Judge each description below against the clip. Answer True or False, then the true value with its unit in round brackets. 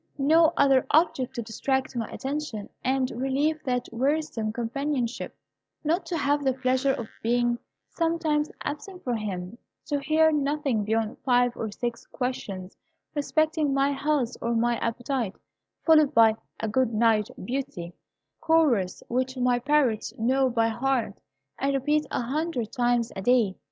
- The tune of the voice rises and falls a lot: False (4.0 semitones)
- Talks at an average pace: True (145 wpm)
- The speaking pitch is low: False (260 Hz)